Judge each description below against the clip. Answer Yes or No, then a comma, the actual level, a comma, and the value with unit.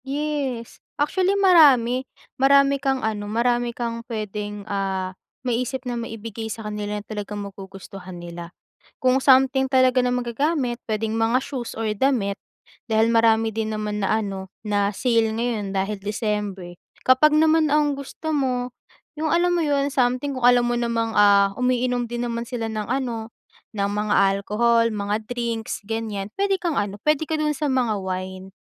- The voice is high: Yes, high, 230 Hz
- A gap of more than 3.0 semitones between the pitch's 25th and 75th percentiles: Yes, average, 4.0 semitones